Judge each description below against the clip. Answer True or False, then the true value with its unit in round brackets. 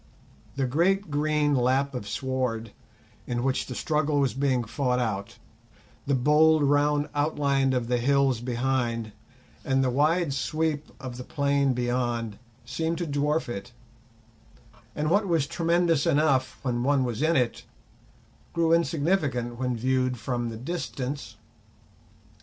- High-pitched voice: False (135 Hz)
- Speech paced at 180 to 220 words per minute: False (135 wpm)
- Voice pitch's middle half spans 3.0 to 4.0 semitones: True (3.4 semitones)